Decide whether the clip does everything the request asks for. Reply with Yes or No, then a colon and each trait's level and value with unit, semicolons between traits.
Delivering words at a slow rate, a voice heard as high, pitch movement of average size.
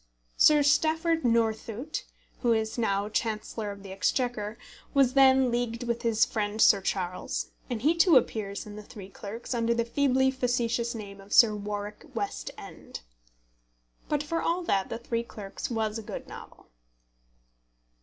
No: average, 155 wpm; high, 230 Hz; average, 3.6 semitones